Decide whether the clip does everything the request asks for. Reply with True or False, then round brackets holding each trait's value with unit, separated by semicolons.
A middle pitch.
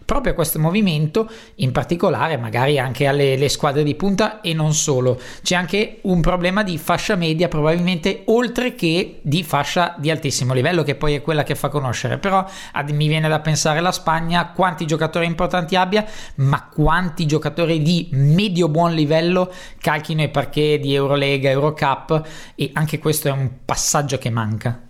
True (160 Hz)